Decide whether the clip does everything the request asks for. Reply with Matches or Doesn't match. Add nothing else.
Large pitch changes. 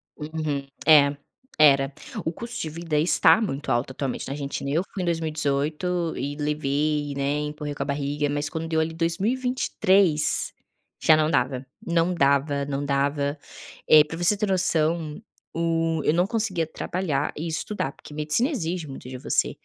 Doesn't match